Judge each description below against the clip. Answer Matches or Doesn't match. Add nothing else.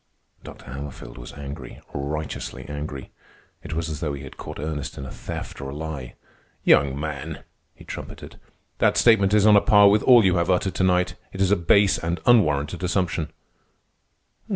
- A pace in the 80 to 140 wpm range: Doesn't match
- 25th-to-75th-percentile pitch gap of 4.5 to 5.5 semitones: Matches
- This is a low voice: Matches